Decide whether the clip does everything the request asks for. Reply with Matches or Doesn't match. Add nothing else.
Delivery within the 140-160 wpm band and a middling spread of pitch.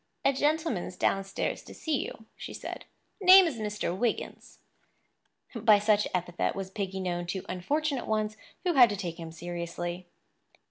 Doesn't match